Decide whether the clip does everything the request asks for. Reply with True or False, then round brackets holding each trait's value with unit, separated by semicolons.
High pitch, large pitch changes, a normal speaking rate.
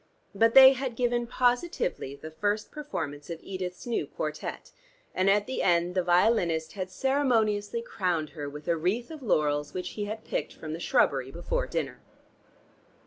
True (195 Hz; 6.4 semitones; 165 wpm)